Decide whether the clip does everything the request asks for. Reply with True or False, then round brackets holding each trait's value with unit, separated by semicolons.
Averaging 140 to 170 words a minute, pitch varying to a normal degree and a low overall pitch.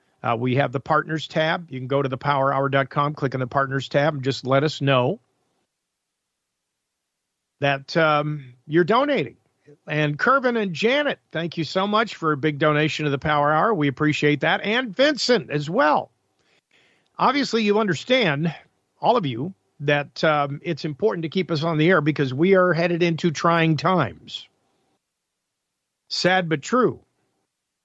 False (160 wpm; 3.8 semitones; 155 Hz)